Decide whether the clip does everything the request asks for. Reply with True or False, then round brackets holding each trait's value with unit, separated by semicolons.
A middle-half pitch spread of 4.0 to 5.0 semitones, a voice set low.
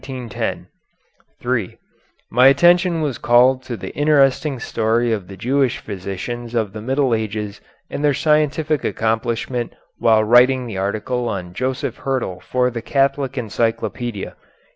False (3.5 semitones; 120 Hz)